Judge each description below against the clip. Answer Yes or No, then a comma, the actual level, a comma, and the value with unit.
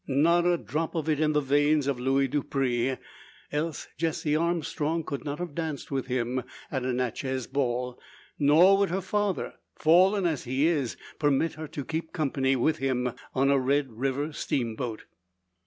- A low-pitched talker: No, medium, 145 Hz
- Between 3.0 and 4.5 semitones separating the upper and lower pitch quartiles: Yes, average, 3.5 semitones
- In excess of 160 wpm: Yes, average, 170 wpm